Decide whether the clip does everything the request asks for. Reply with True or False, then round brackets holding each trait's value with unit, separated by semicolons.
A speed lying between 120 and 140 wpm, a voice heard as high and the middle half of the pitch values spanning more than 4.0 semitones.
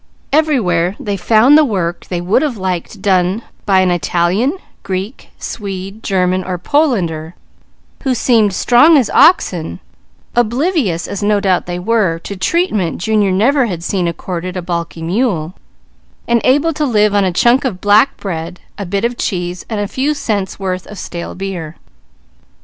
False (160 wpm; 195 Hz; 5.0 semitones)